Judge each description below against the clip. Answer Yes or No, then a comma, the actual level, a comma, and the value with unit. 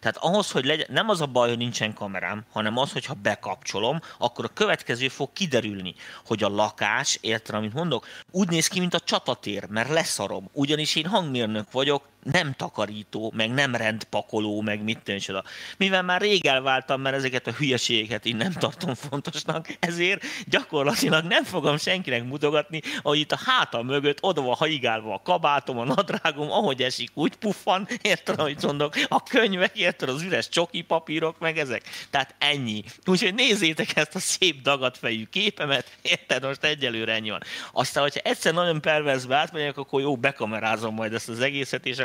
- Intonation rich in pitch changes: Yes, wide, 6.4 semitones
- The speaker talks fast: Yes, fast, 170 wpm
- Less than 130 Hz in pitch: No, medium, 140 Hz